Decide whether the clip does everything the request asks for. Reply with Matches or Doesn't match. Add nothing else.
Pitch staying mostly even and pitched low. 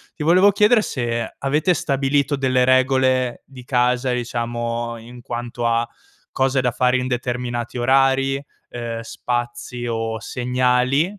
Matches